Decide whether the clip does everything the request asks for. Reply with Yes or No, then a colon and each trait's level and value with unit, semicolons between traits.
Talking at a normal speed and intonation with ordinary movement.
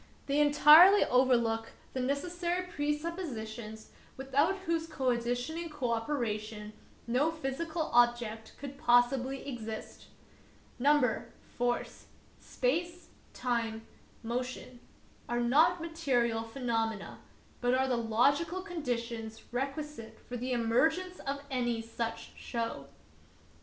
No: slow, 100 wpm; average, 4.4 semitones